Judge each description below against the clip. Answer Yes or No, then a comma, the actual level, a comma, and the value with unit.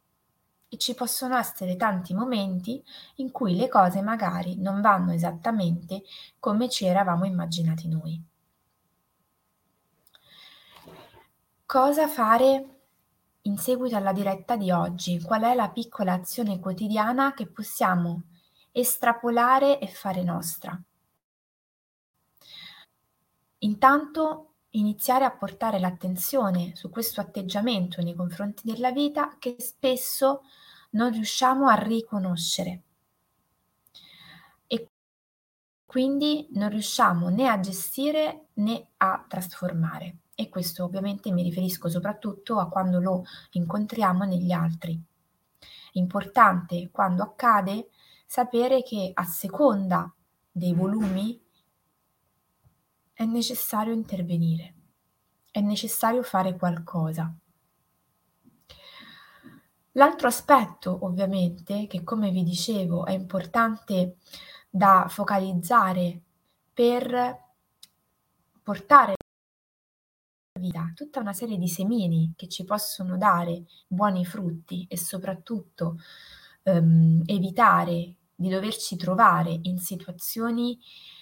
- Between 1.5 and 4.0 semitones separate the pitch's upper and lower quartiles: No, average, 4.5 semitones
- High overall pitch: Yes, high, 195 Hz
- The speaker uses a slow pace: Yes, slow, 95 wpm